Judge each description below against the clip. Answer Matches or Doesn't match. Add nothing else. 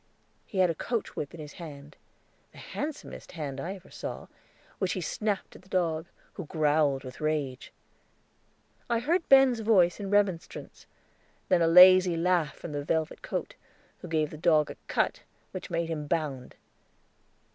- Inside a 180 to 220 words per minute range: Doesn't match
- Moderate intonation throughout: Matches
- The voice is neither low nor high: Matches